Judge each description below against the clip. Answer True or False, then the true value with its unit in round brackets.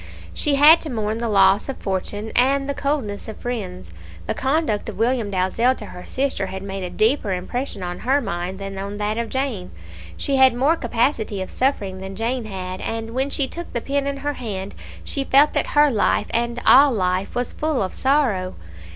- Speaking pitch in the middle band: False (230 Hz)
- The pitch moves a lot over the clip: True (5.7 semitones)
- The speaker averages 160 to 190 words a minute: False (205 wpm)